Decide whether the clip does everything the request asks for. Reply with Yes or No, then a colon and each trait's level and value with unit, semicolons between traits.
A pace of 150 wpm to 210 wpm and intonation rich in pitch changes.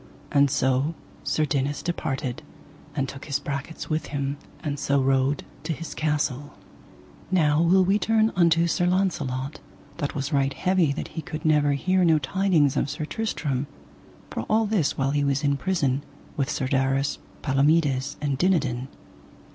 No: average, 160 wpm; average, 3.4 semitones